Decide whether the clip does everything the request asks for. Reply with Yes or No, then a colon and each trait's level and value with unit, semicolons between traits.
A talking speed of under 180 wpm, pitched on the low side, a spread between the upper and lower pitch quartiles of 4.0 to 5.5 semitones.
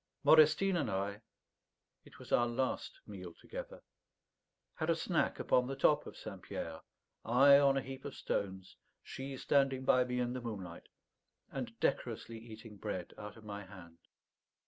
Yes: average, 160 wpm; low, 125 Hz; average, 5.1 semitones